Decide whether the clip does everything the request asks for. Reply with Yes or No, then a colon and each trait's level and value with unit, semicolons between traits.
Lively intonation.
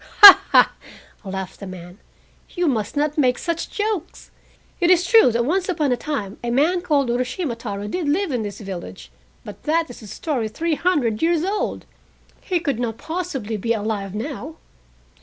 Yes: wide, 7.7 semitones